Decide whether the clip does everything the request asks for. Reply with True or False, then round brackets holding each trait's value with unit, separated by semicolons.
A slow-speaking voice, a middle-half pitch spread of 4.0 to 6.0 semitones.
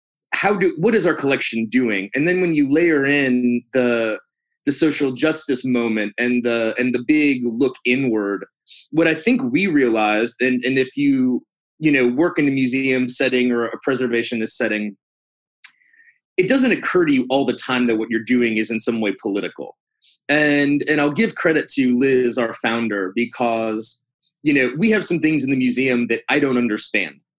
False (185 wpm; 4.6 semitones)